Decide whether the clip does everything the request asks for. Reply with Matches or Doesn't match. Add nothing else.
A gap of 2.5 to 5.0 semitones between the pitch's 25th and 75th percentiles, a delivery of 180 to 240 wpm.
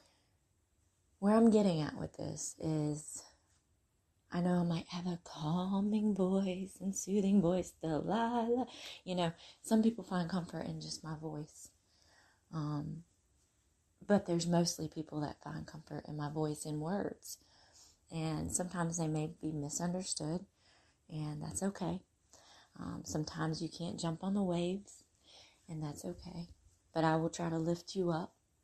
Doesn't match